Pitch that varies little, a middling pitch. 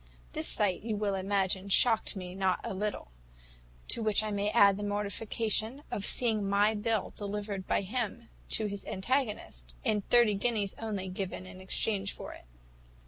No: narrow, 2.0 semitones; high, 205 Hz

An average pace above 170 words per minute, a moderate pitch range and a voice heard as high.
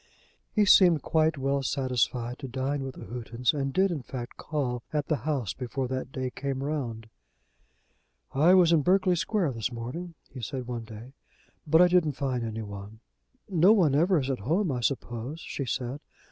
No: average, 180 wpm; average, 4.5 semitones; low, 135 Hz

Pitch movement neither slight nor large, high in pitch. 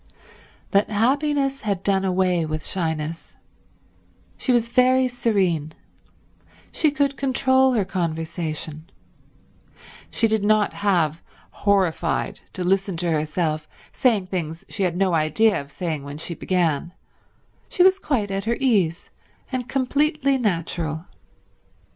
No: wide, 7.0 semitones; high, 195 Hz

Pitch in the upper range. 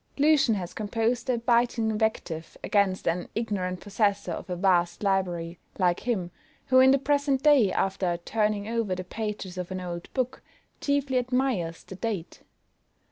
Yes: high, 210 Hz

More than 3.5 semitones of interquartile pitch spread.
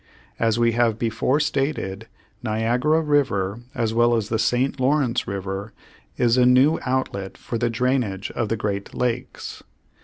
No: average, 2.8 semitones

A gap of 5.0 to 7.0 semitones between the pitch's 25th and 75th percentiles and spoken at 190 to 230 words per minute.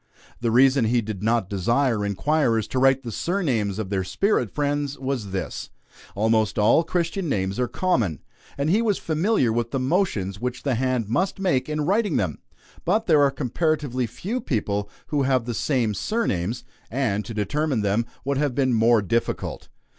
No: wide, 5.5 semitones; average, 175 wpm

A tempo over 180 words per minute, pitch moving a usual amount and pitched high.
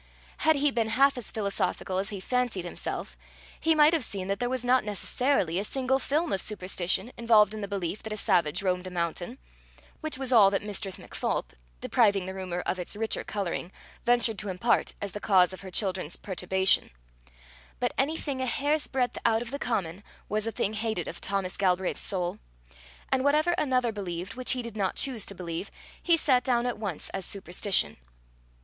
Yes: average, 195 wpm; average, 4.9 semitones; high, 210 Hz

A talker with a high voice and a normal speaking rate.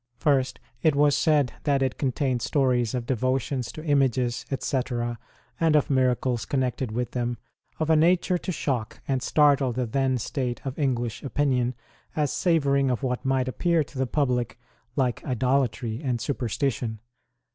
No: low, 130 Hz; average, 155 wpm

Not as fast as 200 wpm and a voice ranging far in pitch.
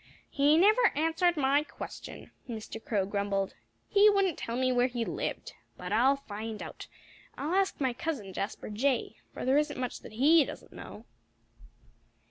Yes: average, 160 wpm; wide, 6.3 semitones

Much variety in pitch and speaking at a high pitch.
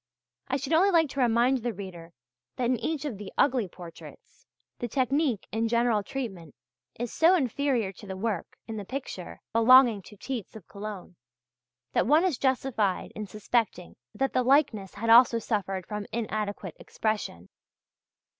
No: average, 4.6 semitones; high, 230 Hz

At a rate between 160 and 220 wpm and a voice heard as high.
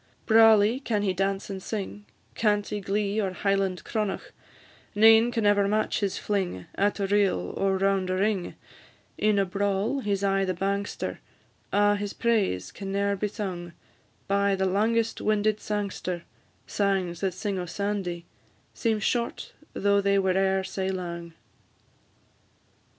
No: average, 150 wpm; high, 200 Hz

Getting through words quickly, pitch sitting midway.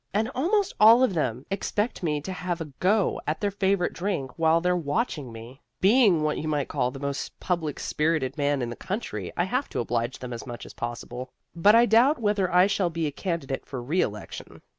Yes: fast, 210 wpm; medium, 165 Hz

